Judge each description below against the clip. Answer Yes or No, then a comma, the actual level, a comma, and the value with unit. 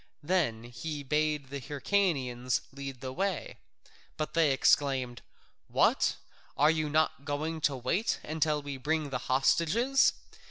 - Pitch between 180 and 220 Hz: No, medium, 145 Hz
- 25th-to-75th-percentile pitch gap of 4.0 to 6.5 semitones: No, average, 3.2 semitones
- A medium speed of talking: No, slow, 130 wpm